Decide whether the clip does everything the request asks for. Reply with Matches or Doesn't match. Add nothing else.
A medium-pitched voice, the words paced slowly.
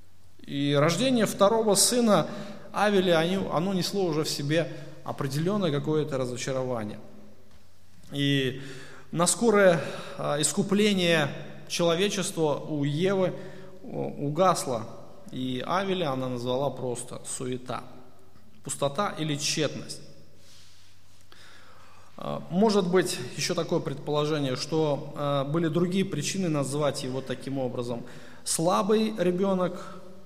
Matches